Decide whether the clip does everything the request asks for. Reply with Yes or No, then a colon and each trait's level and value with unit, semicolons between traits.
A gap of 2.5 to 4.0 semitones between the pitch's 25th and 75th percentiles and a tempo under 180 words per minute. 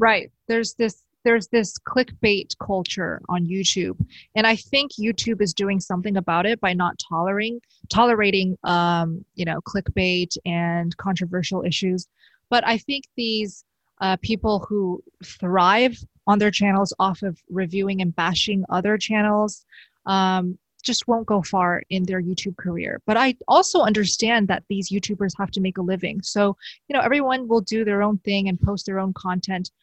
Yes: average, 3.4 semitones; average, 165 wpm